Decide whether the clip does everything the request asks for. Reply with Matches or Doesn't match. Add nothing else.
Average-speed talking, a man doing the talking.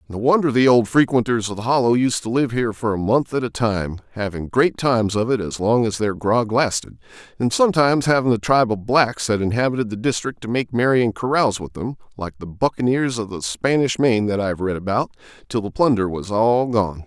Doesn't match